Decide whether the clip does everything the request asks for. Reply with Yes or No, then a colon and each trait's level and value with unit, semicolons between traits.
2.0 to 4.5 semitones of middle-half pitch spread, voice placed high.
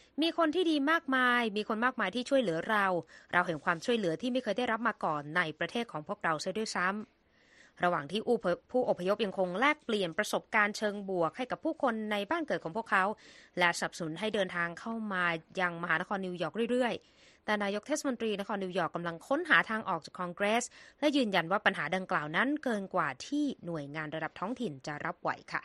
No: average, 5.3 semitones; high, 200 Hz